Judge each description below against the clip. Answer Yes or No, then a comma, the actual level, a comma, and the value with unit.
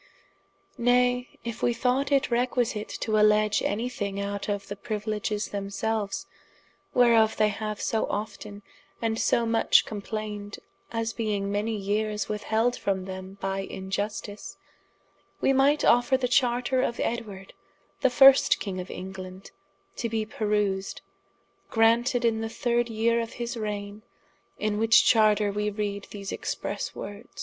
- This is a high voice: Yes, high, 215 Hz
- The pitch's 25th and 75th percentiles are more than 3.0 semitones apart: No, narrow, 2.5 semitones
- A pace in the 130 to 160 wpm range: Yes, average, 140 wpm